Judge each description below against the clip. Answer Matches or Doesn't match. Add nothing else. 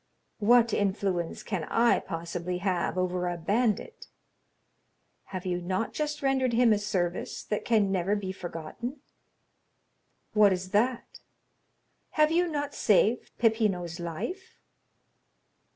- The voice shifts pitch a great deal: Doesn't match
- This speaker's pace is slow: Matches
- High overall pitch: Matches